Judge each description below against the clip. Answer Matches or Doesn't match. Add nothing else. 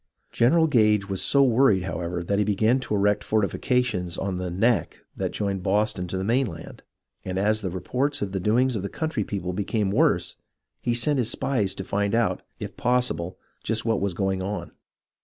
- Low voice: Matches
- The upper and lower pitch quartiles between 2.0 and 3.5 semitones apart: Doesn't match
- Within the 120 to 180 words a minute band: Doesn't match